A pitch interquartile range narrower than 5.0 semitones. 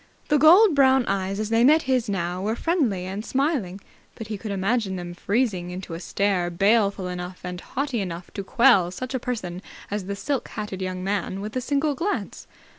No: wide, 5.6 semitones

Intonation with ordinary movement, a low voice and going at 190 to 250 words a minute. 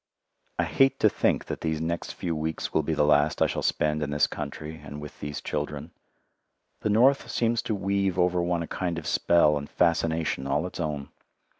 Yes: average, 3.3 semitones; very low, 80 Hz; average, 200 wpm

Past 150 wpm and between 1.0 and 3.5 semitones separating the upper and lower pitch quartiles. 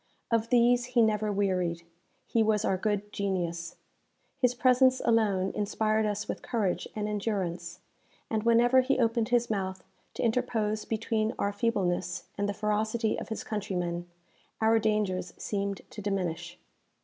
No: average, 145 wpm; average, 3.1 semitones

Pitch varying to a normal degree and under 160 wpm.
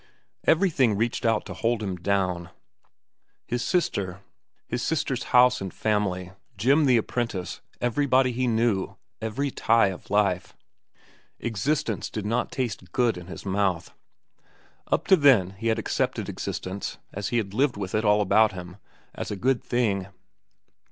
Yes: average, 4.2 semitones; average, 145 wpm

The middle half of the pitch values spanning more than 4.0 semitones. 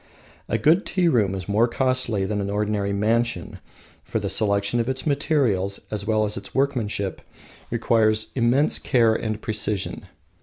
No: average, 3.7 semitones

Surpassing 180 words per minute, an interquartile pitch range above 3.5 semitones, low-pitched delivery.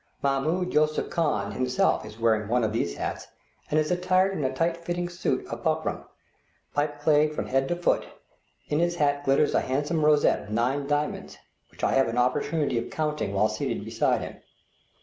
No: average, 190 wpm; average, 4.3 semitones; medium, 145 Hz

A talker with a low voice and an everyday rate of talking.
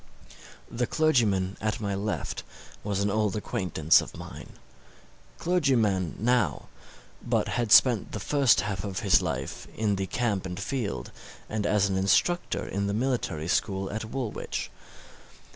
Yes: low, 105 Hz; average, 145 wpm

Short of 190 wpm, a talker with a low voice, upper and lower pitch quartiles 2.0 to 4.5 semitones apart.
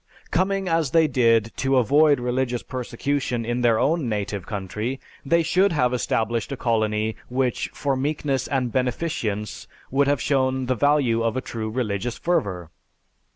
Yes: average, 155 wpm; low, 125 Hz; average, 3.9 semitones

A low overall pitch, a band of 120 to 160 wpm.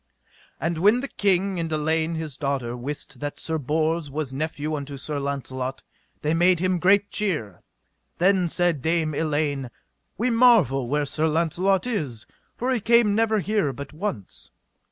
No: medium, 160 Hz; average, 155 wpm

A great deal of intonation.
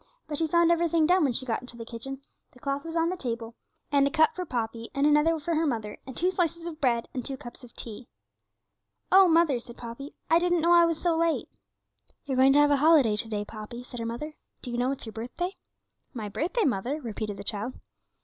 Yes: wide, 5.8 semitones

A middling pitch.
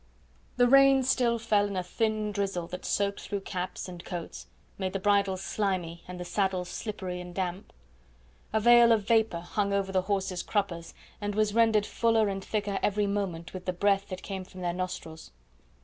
No: high, 200 Hz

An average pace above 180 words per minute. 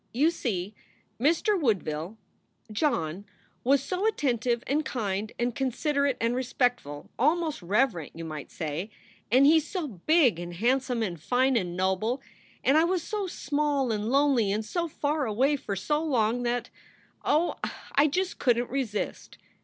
No: average, 155 wpm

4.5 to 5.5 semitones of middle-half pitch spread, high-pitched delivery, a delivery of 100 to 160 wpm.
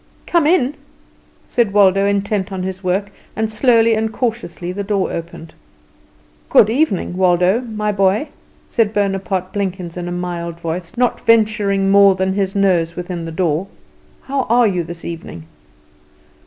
No: average, 3.4 semitones; high, 195 Hz; average, 150 wpm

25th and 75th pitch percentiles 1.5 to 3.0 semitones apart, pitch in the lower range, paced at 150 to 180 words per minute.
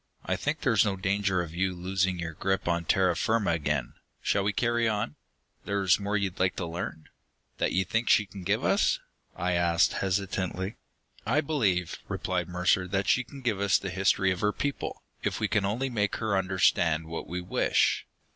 No: average, 2.7 semitones; very low, 95 Hz; average, 190 wpm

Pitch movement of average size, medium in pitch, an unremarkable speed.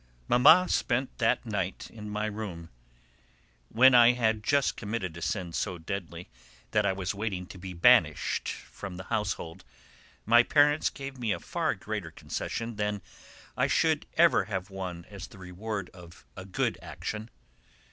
No: average, 3.8 semitones; low, 105 Hz; average, 155 wpm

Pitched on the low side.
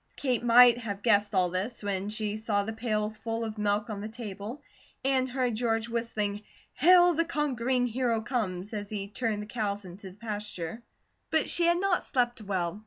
No: high, 220 Hz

